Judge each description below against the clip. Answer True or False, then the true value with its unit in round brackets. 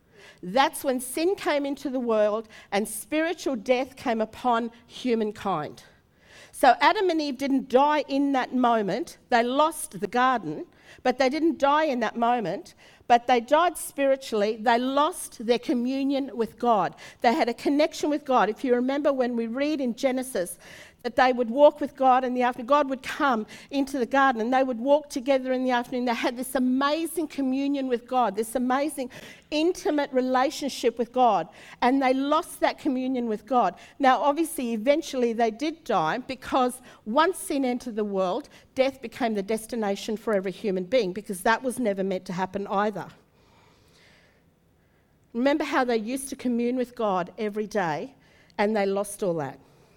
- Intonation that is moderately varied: True (3.4 semitones)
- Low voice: False (255 Hz)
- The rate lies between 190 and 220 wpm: False (170 wpm)